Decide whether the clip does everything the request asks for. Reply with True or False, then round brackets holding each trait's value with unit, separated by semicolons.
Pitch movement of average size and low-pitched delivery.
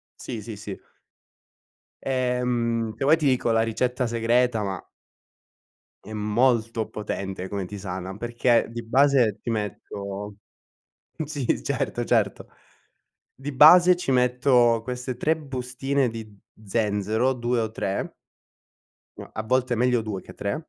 True (3.1 semitones; 120 Hz)